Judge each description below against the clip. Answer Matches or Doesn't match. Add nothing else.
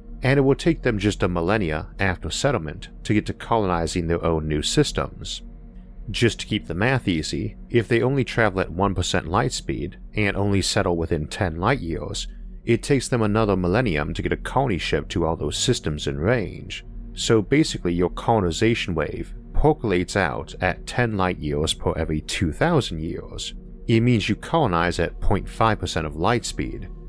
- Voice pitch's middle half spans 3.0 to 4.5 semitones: Doesn't match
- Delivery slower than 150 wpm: Doesn't match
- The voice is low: Matches